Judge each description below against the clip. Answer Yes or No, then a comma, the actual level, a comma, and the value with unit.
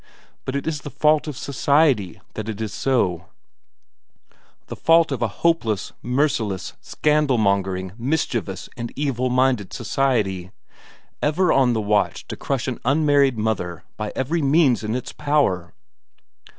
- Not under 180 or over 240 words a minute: No, slow, 135 wpm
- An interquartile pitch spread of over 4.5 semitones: Yes, wide, 5.6 semitones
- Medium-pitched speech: No, low, 125 Hz